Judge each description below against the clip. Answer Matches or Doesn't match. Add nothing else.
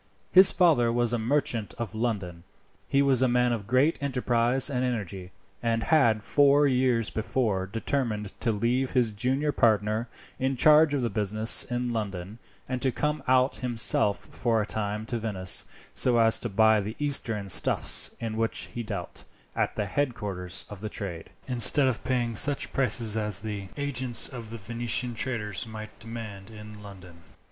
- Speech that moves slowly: Doesn't match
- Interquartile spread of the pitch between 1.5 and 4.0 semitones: Matches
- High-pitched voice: Doesn't match